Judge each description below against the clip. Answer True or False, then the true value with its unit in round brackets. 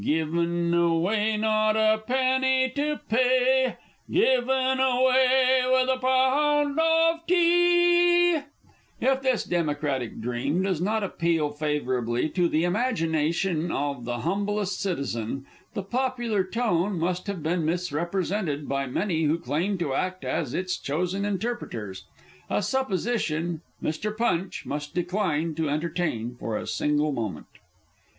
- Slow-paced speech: True (125 wpm)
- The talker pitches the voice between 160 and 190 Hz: True (185 Hz)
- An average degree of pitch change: False (8.5 semitones)